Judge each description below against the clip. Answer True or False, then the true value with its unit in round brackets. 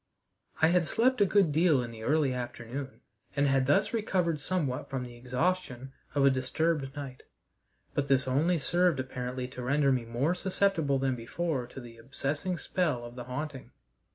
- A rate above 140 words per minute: True (175 wpm)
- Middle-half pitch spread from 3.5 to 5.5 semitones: True (4.6 semitones)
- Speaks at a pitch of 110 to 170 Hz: True (140 Hz)